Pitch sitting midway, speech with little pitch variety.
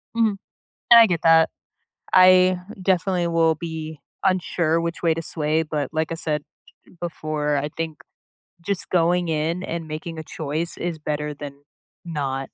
Yes: medium, 165 Hz; narrow, 2.3 semitones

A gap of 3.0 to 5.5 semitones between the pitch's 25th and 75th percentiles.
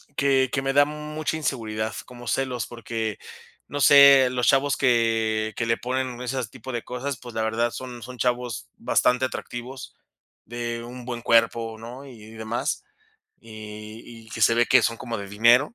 No: narrow, 2.4 semitones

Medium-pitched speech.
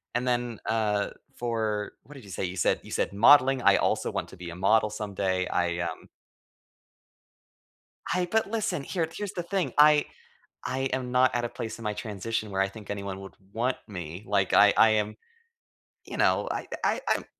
No: low, 110 Hz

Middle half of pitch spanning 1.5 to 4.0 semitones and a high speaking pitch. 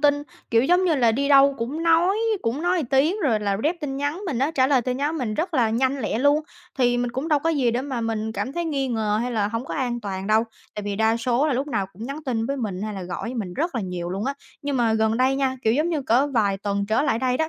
No: average, 4.5 semitones; very high, 250 Hz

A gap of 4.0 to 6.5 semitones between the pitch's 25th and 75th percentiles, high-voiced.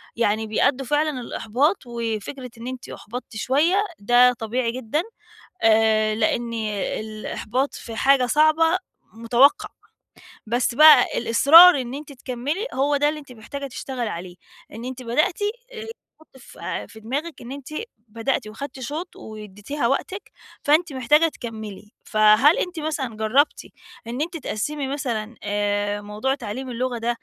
Yes: average, 4.6 semitones; very high, 250 Hz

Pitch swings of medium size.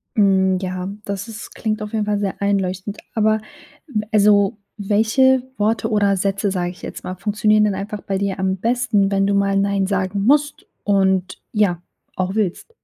No: narrow, 1.8 semitones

